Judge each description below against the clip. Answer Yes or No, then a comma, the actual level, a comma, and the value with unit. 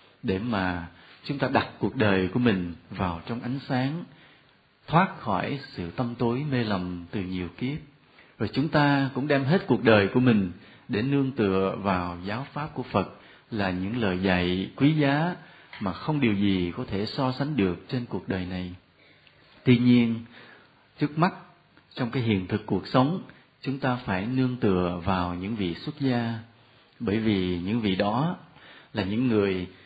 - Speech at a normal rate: Yes, average, 175 wpm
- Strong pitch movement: Yes, wide, 6.0 semitones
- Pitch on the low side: Yes, low, 115 Hz